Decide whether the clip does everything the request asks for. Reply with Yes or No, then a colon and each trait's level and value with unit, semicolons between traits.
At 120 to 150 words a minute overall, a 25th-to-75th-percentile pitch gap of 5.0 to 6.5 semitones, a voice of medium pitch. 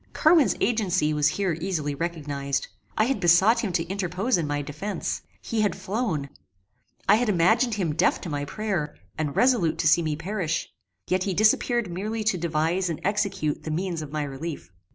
No: average, 180 wpm; wide, 5.4 semitones; medium, 175 Hz